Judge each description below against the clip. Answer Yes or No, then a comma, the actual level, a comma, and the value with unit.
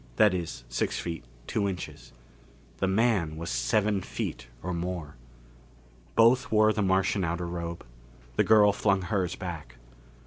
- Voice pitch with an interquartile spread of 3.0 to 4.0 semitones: Yes, average, 3.6 semitones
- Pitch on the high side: No, very low, 90 Hz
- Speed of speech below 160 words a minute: Yes, average, 140 wpm